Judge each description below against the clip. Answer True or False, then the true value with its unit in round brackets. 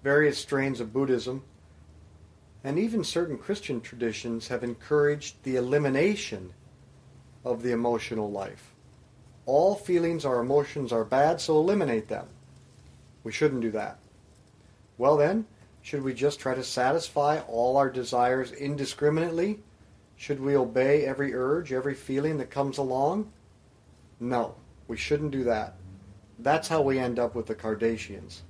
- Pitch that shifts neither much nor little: True (4.3 semitones)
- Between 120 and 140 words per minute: True (135 wpm)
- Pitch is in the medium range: False (130 Hz)